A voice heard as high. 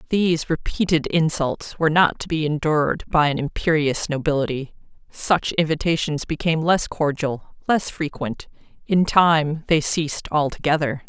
No: medium, 155 Hz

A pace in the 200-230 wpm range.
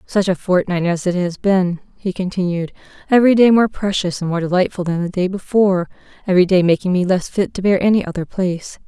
Yes: fast, 205 wpm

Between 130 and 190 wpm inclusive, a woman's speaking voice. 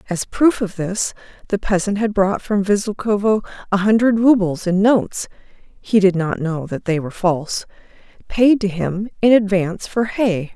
Yes: average, 170 wpm; female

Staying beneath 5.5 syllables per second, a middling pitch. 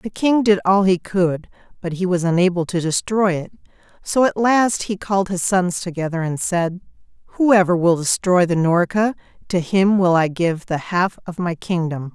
Yes: 4.6 syllables/s; medium, 180 Hz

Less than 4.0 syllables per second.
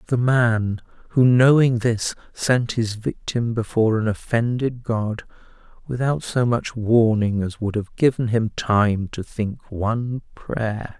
Yes: 3.8 syllables/s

